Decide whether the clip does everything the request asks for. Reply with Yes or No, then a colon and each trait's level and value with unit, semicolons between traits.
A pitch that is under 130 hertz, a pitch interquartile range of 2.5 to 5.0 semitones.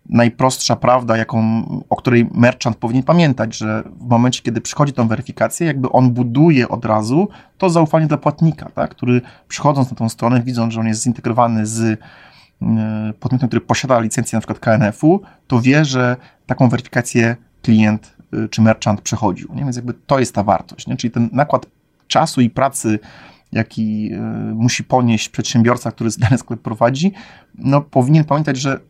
Yes: low, 120 Hz; average, 3.2 semitones